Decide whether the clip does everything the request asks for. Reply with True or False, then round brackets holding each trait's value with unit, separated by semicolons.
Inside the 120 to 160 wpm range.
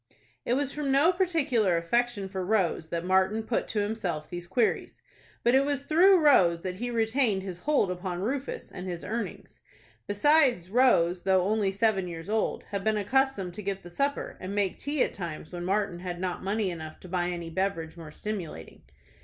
False (190 wpm)